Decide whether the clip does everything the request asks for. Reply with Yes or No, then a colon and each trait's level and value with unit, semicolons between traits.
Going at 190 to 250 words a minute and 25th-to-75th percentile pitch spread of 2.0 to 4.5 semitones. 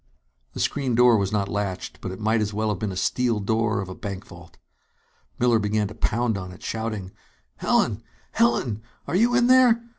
Yes: average, 200 wpm; average, 3.4 semitones